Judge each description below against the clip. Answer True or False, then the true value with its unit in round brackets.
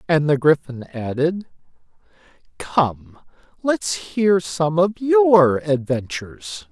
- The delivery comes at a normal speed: False (100 wpm)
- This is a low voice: False (160 Hz)